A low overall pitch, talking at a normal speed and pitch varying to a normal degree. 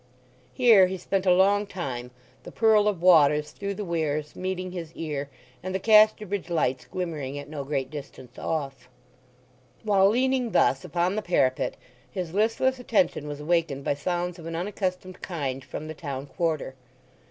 No: medium, 175 Hz; average, 165 wpm; average, 5.0 semitones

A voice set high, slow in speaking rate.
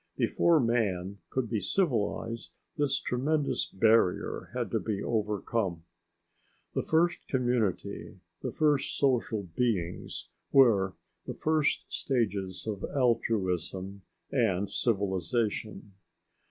No: low, 110 Hz; slow, 100 wpm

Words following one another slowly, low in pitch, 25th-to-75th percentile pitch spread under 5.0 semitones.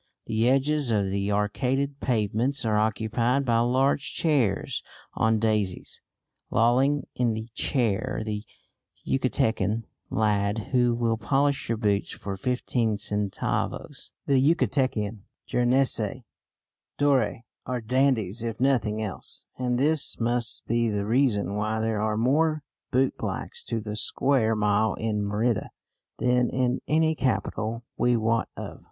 Yes: slow, 125 wpm; low, 115 Hz; average, 3.4 semitones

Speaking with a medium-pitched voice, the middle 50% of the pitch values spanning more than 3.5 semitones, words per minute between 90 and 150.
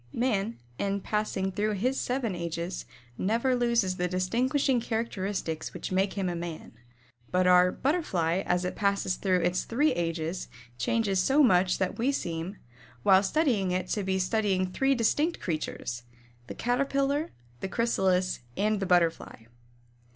No: high, 195 Hz; average, 4.6 semitones; average, 145 wpm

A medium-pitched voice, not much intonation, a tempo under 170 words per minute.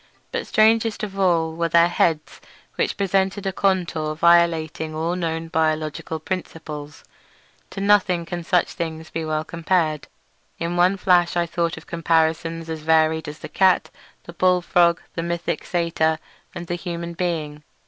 Yes: medium, 170 Hz; narrow, 1.8 semitones; average, 150 wpm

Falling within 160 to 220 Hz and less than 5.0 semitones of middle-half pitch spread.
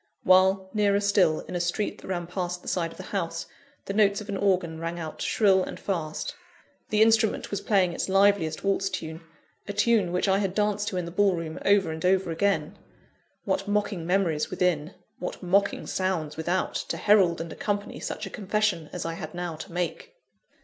Yes: medium, 185 Hz; average, 3.0 semitones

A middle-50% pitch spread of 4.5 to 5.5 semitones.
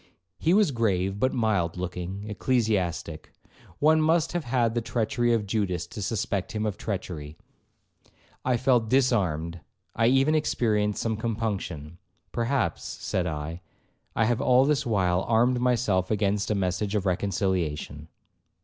Yes: average, 4.8 semitones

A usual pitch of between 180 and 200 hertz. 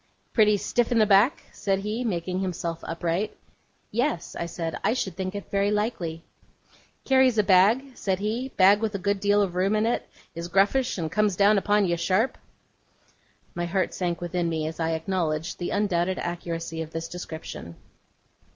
Yes: high, 190 Hz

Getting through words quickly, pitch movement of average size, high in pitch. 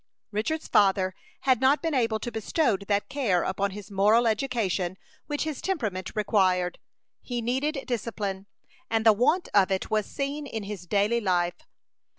No: average, 160 wpm; average, 4.9 semitones; high, 215 Hz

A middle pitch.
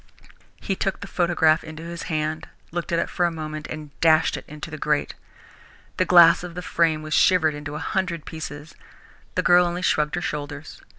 Yes: medium, 160 Hz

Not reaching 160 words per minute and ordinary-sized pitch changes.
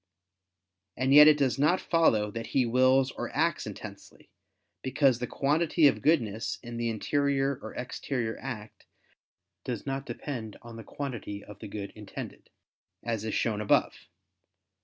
Yes: average, 150 wpm; average, 3.9 semitones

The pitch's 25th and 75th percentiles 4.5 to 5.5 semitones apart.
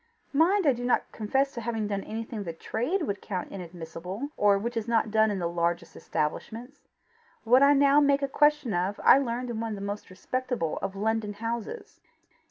Yes: average, 5.0 semitones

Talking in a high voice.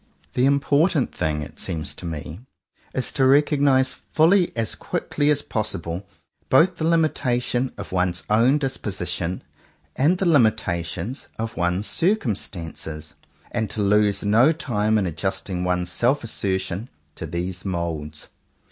No: low, 105 Hz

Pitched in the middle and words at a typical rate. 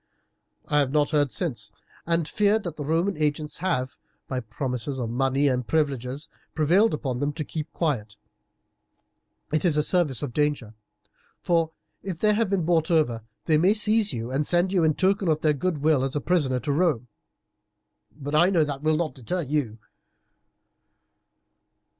Yes: medium, 150 Hz; average, 170 wpm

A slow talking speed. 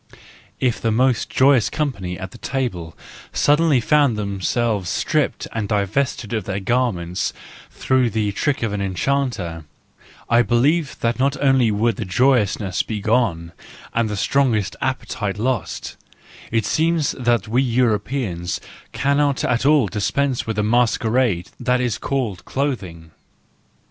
Yes: slow, 130 wpm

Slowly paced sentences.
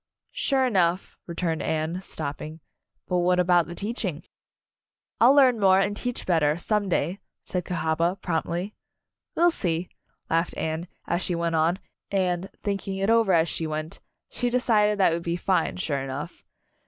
No: average, 165 wpm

